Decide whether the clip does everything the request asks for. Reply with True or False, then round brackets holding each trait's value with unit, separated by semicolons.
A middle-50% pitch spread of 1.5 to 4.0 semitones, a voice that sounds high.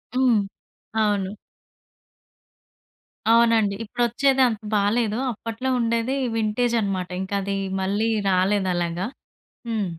True (2.9 semitones; 215 Hz)